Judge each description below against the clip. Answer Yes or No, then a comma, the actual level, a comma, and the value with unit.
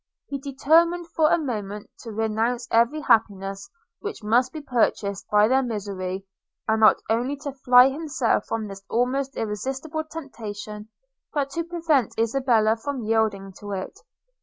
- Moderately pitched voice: No, high, 235 Hz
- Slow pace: No, average, 145 wpm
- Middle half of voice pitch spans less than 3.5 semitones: No, average, 4.8 semitones